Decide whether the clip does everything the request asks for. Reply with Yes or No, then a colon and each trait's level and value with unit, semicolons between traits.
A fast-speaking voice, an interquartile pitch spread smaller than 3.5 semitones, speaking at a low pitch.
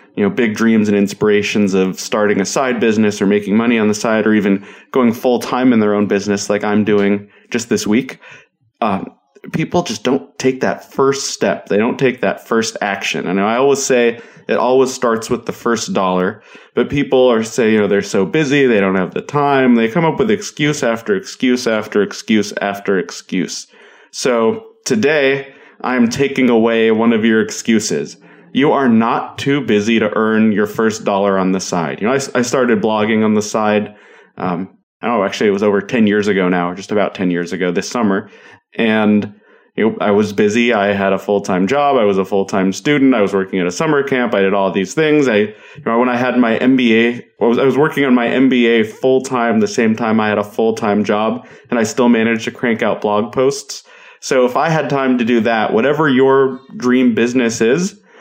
No: fast, 215 wpm; average, 4.0 semitones; low, 115 Hz